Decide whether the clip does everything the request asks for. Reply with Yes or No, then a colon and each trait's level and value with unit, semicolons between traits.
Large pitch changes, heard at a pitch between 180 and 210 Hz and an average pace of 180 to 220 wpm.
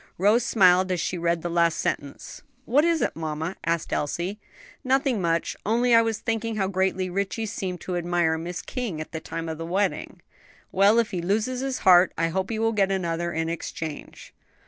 No: average, 4.6 semitones; medium, 185 Hz; average, 195 wpm